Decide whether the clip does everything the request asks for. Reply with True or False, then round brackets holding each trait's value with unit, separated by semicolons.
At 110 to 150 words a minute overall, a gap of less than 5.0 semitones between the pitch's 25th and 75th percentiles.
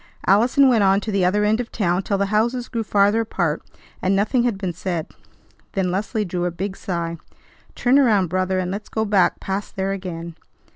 False (200 wpm; 2.9 semitones)